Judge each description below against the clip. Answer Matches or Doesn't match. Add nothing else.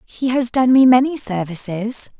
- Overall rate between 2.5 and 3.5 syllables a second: Doesn't match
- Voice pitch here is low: Doesn't match